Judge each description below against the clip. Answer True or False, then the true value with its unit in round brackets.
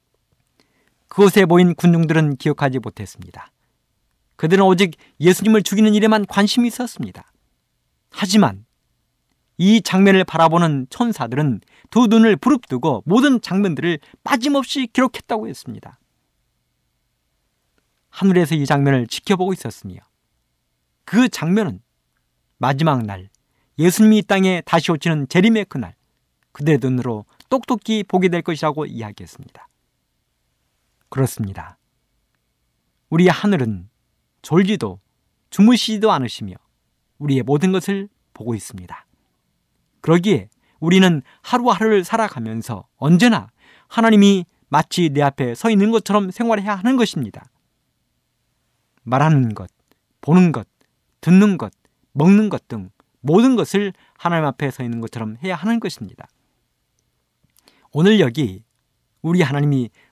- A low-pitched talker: False (160 Hz)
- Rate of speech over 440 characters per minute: False (275 characters per minute)